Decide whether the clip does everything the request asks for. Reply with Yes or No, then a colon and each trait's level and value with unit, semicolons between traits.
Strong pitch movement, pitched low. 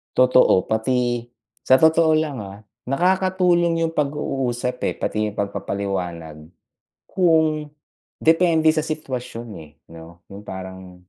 Yes: wide, 8.3 semitones; low, 130 Hz